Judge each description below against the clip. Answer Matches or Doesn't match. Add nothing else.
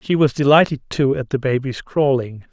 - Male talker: Matches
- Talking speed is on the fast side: Doesn't match